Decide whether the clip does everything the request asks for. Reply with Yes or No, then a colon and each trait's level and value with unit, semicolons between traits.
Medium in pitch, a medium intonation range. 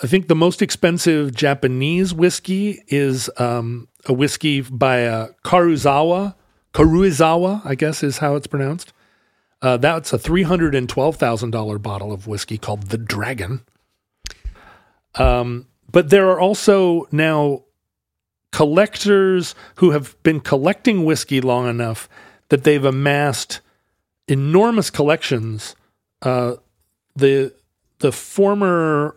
No: medium, 145 Hz; wide, 5.9 semitones